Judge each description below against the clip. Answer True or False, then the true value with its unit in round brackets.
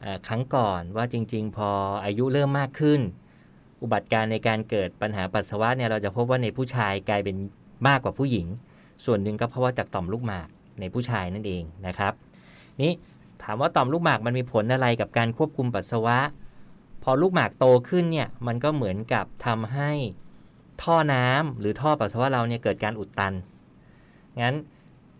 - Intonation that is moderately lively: True (3.9 semitones)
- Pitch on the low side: True (120 Hz)